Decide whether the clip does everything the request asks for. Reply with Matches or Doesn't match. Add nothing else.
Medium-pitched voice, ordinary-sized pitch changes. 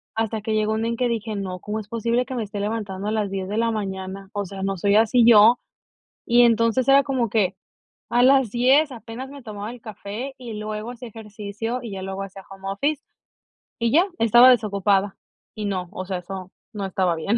Doesn't match